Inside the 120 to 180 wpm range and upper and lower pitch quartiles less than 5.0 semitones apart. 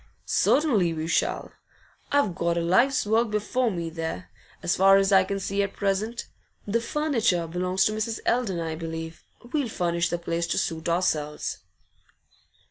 Yes: average, 160 wpm; average, 4.5 semitones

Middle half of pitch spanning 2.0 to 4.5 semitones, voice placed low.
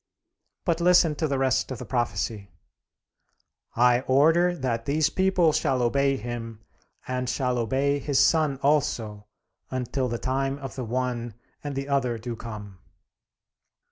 Yes: average, 3.1 semitones; low, 130 Hz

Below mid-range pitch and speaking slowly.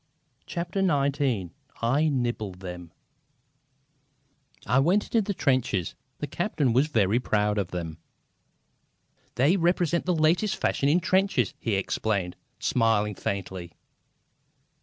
Yes: low, 125 Hz; slow, 115 wpm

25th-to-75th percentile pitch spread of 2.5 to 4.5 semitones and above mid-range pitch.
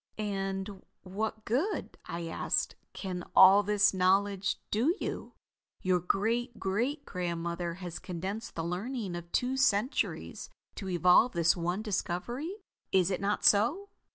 Yes: average, 3.6 semitones; high, 195 Hz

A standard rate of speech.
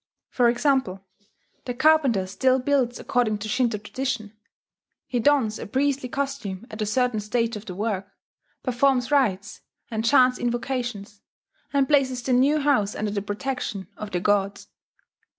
Yes: average, 150 wpm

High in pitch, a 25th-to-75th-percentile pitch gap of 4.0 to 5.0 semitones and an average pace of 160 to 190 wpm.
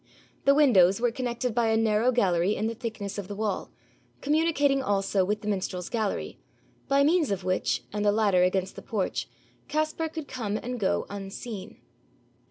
Yes: high, 220 Hz; average, 4.4 semitones; average, 175 wpm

